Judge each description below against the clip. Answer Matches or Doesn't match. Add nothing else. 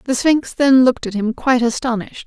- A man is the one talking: Doesn't match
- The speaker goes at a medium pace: Doesn't match